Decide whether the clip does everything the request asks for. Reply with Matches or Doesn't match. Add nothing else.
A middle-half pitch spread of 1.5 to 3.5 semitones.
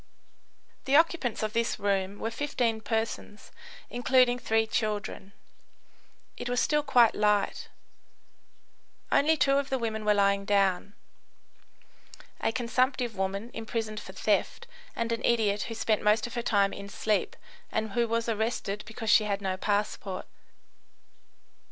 Matches